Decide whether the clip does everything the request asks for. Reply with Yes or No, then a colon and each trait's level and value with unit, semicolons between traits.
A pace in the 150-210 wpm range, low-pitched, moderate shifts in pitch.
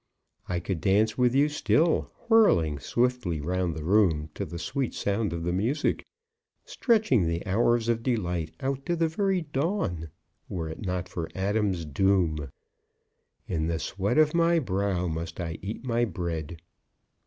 No: average, 155 wpm; very low, 95 Hz; wide, 7.0 semitones